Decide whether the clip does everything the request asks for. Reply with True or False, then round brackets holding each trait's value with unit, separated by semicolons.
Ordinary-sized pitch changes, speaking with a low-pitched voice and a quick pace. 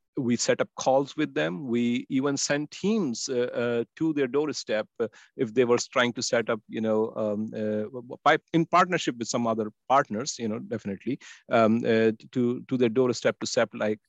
False (3.6 semitones; 120 Hz; 185 wpm)